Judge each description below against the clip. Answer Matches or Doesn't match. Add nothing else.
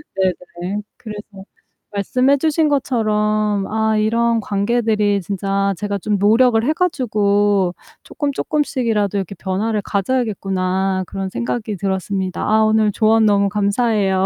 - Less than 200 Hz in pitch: Doesn't match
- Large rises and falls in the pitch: Doesn't match